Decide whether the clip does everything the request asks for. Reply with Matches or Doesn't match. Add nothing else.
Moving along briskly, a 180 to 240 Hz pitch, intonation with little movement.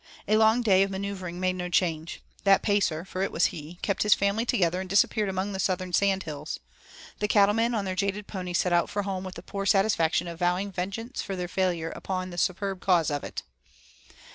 Matches